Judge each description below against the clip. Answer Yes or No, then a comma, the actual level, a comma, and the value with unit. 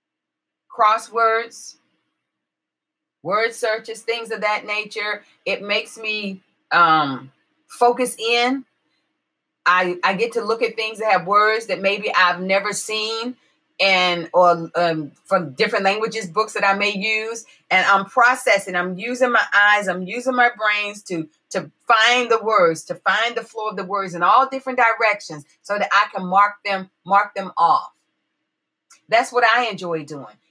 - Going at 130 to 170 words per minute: Yes, average, 155 wpm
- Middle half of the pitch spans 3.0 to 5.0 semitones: Yes, average, 3.5 semitones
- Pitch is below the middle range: No, high, 210 Hz